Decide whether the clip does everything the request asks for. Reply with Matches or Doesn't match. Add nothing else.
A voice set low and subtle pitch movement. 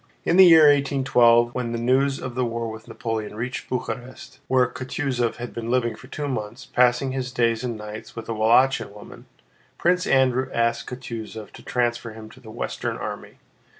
Matches